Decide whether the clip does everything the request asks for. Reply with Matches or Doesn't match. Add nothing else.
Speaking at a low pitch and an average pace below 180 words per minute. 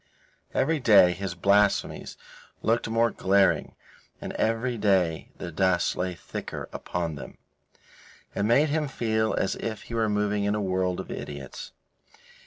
Matches